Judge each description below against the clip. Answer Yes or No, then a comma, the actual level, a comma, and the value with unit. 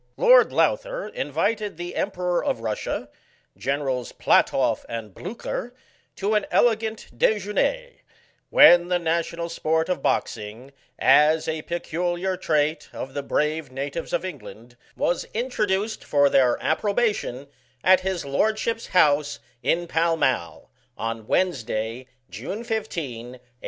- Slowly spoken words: Yes, slow, 120 wpm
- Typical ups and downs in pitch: No, wide, 7.0 semitones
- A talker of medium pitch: Yes, medium, 170 Hz